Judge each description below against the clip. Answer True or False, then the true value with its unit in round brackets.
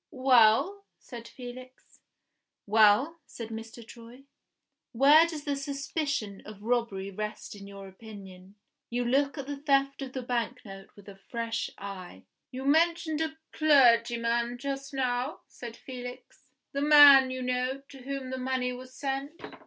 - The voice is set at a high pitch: True (250 Hz)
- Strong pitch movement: False (3.4 semitones)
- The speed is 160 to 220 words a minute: False (145 wpm)